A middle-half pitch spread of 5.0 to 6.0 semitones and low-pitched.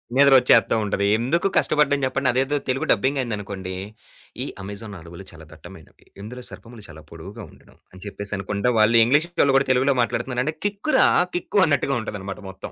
Yes: wide, 5.4 semitones; low, 115 Hz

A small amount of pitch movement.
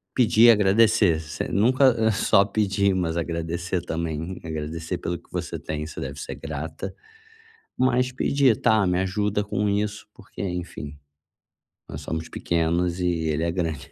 No: average, 4.2 semitones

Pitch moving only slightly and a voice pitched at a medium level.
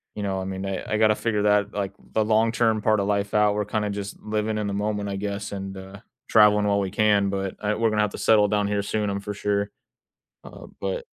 No: narrow, 1.1 semitones; low, 105 Hz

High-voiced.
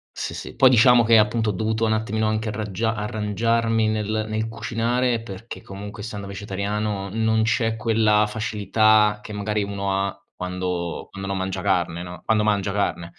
No: low, 105 Hz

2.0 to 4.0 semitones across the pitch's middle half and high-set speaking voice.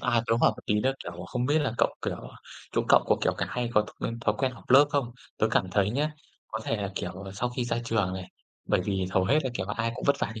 No: average, 3.7 semitones; low, 115 Hz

